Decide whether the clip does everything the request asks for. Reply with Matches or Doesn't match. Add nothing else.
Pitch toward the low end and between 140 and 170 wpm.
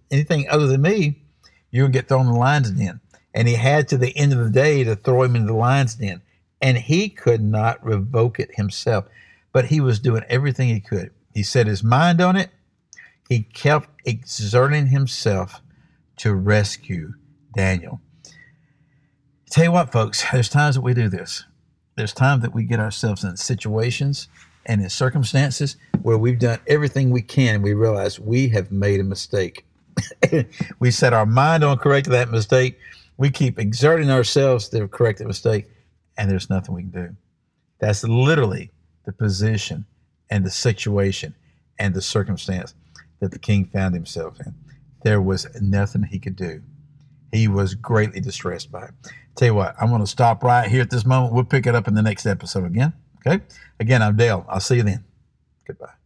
Doesn't match